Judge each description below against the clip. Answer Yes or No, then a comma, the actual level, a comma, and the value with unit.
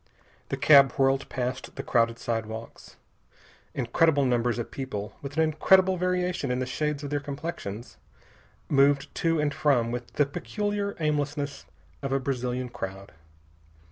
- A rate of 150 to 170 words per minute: No, average, 140 wpm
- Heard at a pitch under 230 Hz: Yes, medium, 140 Hz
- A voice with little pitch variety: No, average, 3.7 semitones